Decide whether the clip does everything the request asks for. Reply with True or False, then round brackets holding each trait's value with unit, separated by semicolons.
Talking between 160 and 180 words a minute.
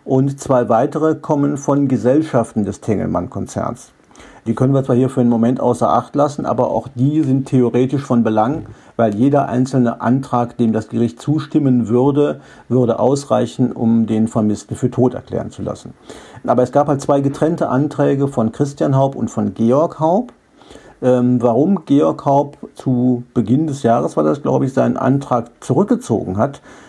True (165 wpm)